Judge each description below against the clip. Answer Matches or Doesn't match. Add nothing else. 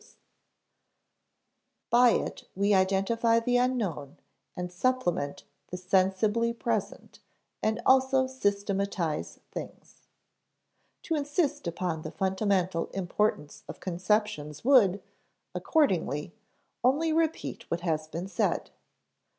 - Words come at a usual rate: Doesn't match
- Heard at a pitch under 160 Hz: Doesn't match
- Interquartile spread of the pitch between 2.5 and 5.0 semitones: Doesn't match